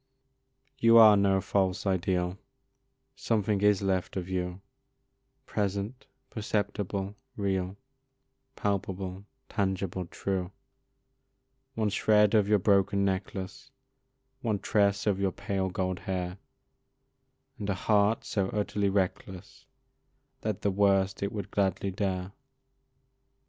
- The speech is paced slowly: Yes, slow, 105 wpm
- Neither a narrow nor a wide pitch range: No, narrow, 1.5 semitones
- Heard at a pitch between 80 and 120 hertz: Yes, low, 100 Hz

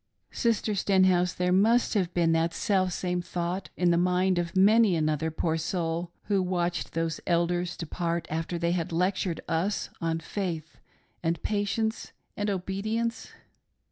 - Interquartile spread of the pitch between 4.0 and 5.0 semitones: No, narrow, 2.5 semitones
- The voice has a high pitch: No, medium, 180 Hz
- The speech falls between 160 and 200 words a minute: No, average, 140 wpm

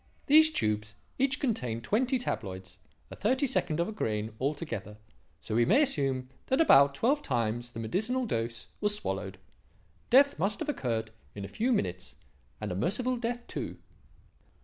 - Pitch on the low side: No, medium, 165 Hz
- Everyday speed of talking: Yes, average, 160 wpm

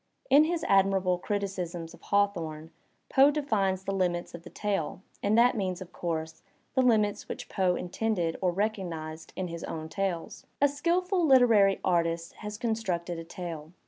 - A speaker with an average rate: Yes, average, 160 wpm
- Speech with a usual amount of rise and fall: Yes, average, 4.3 semitones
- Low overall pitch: No, high, 190 Hz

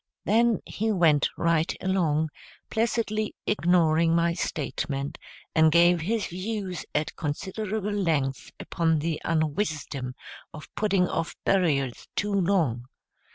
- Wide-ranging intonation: No, average, 4.5 semitones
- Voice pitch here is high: No, medium, 170 Hz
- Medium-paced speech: No, slow, 110 wpm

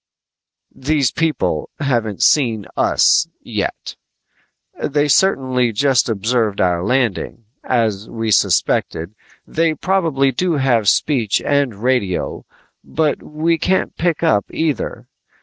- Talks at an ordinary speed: No, slow, 110 wpm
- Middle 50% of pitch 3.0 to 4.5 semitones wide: No, wide, 5.5 semitones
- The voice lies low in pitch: Yes, low, 130 Hz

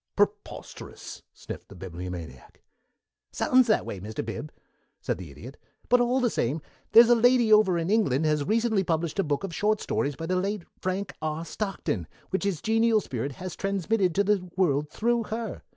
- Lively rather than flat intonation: Yes, wide, 7.0 semitones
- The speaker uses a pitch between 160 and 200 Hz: Yes, medium, 185 Hz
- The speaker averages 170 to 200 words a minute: Yes, average, 180 wpm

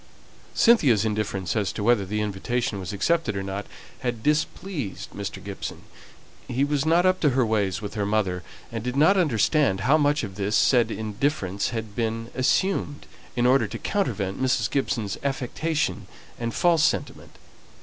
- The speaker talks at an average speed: Yes, average, 160 wpm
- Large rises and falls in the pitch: Yes, wide, 5.8 semitones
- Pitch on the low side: Yes, low, 115 Hz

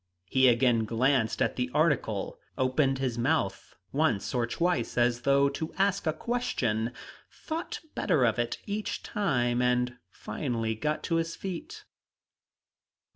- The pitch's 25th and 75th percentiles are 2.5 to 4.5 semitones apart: No, average, 4.9 semitones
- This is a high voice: No, low, 130 Hz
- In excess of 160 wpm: No, slow, 135 wpm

